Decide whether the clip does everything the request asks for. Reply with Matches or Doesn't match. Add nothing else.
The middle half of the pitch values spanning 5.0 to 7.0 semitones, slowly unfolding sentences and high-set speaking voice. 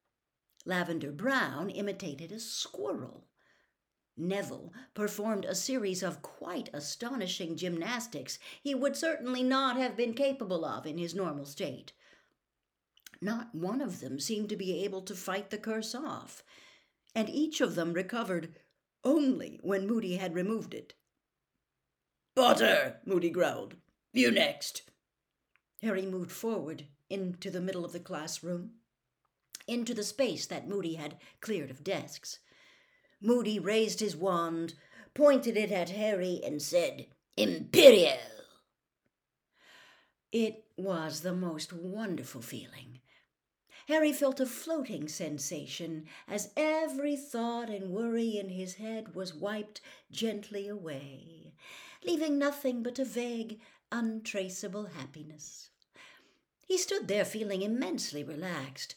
Matches